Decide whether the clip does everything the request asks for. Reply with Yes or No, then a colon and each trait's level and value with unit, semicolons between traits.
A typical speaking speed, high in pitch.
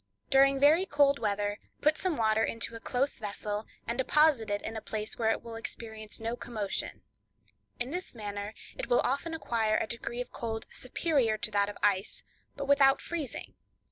Yes: average, 180 wpm; high, 230 Hz